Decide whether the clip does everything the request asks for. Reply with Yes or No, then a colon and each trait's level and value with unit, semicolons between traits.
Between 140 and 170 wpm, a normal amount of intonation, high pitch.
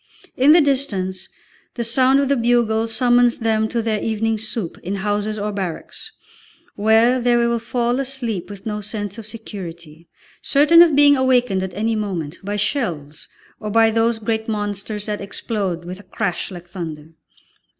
Yes: average, 165 wpm; average, 3.3 semitones; high, 220 Hz